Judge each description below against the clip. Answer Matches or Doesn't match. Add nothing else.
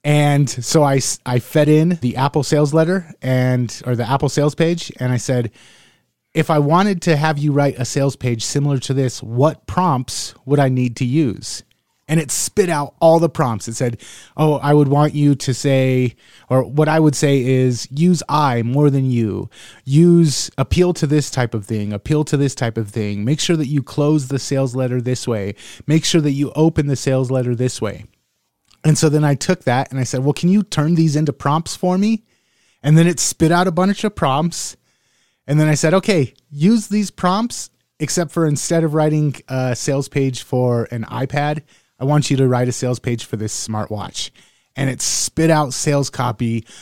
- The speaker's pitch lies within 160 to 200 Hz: Doesn't match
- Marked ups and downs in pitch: Doesn't match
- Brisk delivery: Matches